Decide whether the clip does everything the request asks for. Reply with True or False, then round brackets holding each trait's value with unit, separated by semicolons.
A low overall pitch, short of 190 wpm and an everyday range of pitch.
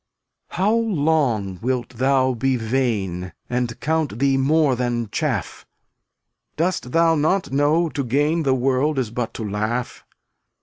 True (130 Hz; 140 wpm; 4.5 semitones)